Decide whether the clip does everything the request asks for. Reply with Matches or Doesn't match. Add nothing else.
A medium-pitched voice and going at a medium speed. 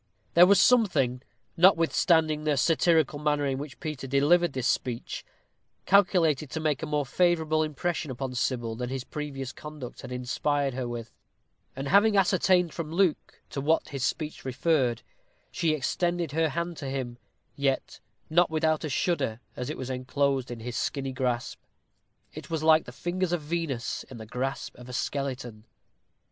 Matches